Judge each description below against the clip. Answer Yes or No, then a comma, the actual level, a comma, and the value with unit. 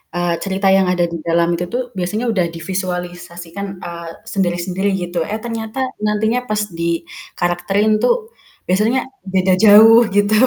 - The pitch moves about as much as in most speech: Yes, average, 3.3 semitones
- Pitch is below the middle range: No, high, 190 Hz